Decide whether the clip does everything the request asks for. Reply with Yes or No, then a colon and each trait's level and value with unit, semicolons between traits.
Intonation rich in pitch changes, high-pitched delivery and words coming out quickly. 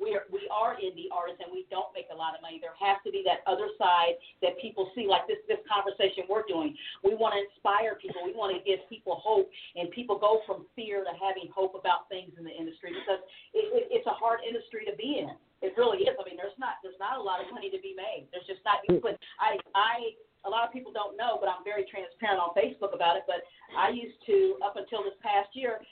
Yes: wide, 7.4 semitones; high, 205 Hz; fast, 250 wpm